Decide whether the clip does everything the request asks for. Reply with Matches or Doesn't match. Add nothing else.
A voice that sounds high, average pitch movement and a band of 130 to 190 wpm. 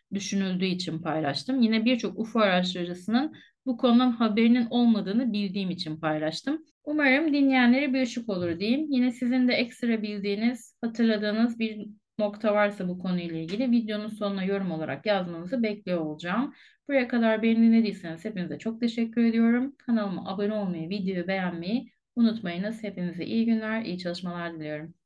Matches